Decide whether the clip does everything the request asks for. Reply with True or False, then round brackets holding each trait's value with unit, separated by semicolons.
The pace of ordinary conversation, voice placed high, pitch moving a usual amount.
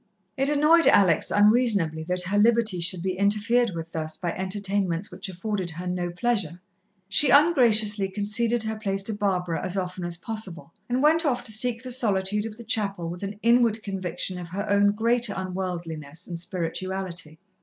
True (175 wpm; 200 Hz; 3.9 semitones)